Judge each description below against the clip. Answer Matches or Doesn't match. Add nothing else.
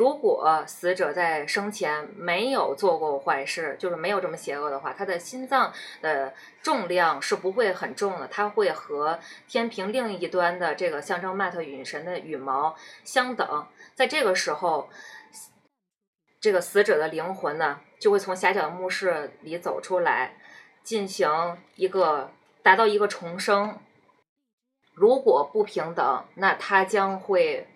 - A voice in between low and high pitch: Doesn't match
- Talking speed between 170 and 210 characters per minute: Doesn't match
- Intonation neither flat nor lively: Doesn't match